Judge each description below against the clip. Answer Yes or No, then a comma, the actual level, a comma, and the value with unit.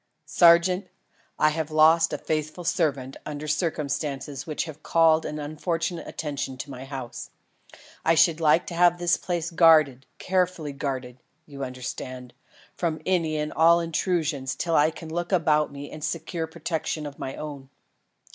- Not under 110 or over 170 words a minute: Yes, average, 155 wpm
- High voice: No, medium, 155 Hz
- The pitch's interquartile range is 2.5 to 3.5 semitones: Yes, average, 2.8 semitones